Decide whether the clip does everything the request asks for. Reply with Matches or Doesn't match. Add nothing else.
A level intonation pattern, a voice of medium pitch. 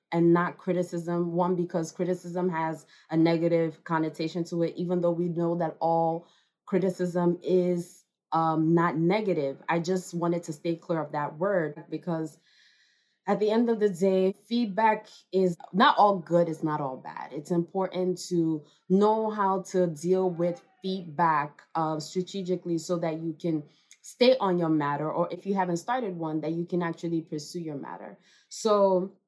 Matches